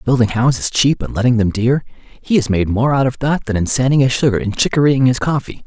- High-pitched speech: No, low, 125 Hz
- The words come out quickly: Yes, fast, 245 wpm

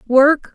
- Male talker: No, female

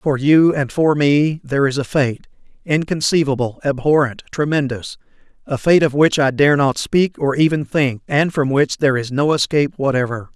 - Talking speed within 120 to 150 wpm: No, average, 170 wpm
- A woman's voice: No, male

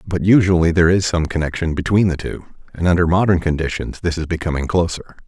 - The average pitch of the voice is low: Yes, very low, 85 Hz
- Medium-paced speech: Yes, average, 195 wpm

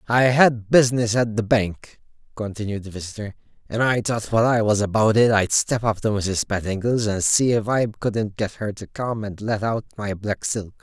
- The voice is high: No, low, 110 Hz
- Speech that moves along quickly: Yes, fast, 210 wpm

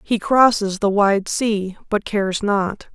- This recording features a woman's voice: Yes, female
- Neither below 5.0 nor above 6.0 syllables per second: No, 3.7 syllables/s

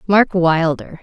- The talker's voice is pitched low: No, medium, 170 Hz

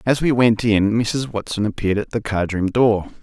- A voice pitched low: Yes, low, 110 Hz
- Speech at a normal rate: No, fast, 225 wpm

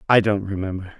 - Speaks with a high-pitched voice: No, low, 100 Hz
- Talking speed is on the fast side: No, average, 180 wpm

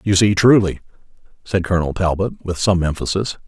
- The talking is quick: No, average, 155 wpm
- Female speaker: No, male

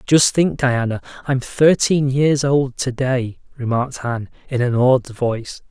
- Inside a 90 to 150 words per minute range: Yes, average, 145 wpm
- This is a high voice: No, low, 130 Hz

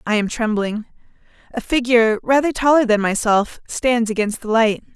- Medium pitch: No, high, 230 Hz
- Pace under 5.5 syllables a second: Yes, 5.1 syllables/s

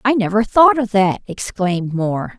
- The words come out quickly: No, average, 175 wpm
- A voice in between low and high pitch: No, high, 210 Hz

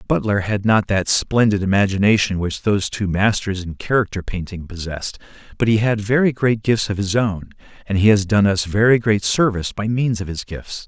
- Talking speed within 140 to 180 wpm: No, average, 200 wpm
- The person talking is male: Yes, male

